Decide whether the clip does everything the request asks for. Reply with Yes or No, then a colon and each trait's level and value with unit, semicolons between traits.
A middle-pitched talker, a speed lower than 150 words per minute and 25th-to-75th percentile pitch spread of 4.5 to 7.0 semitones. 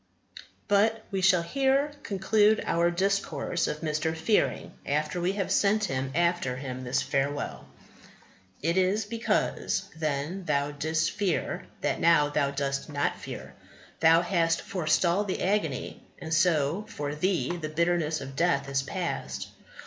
Yes: medium, 165 Hz; average, 140 wpm; average, 4.8 semitones